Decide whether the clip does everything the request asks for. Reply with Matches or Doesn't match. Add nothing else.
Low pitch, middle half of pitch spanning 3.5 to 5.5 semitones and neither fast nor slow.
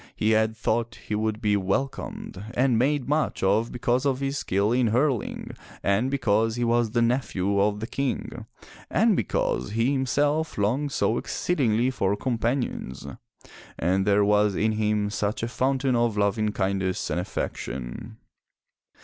Matches